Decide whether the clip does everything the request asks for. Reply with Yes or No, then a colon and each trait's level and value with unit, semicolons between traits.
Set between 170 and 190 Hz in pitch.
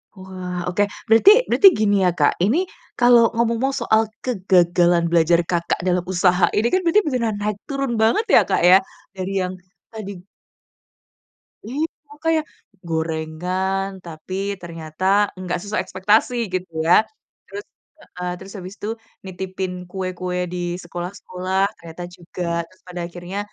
Yes: medium, 185 Hz